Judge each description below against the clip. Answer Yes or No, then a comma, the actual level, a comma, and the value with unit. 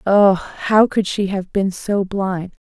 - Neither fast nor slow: Yes, average, 180 wpm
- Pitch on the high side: Yes, high, 195 Hz